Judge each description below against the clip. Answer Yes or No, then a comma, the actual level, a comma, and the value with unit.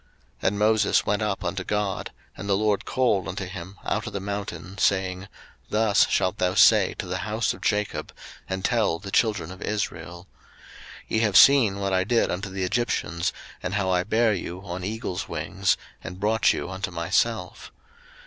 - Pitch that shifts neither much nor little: No, narrow, 2.3 semitones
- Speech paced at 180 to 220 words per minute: Yes, average, 185 wpm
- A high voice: No, low, 100 Hz